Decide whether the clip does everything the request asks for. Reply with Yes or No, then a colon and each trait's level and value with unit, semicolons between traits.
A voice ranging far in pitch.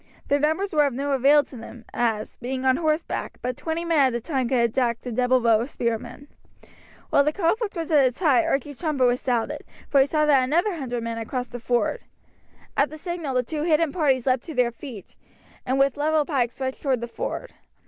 No: average, 3.9 semitones